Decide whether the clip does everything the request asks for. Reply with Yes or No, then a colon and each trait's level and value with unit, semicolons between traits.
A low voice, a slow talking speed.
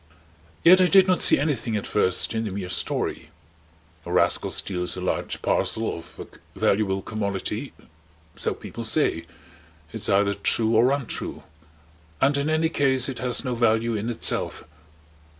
No: low, 115 Hz; average, 155 wpm